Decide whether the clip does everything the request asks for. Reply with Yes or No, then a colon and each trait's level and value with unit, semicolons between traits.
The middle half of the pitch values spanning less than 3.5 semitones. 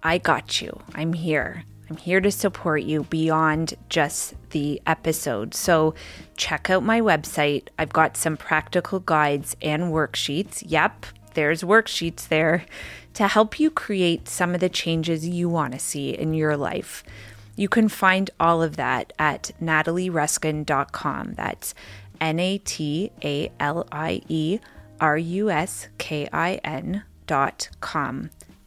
Yes: average, 3.1 semitones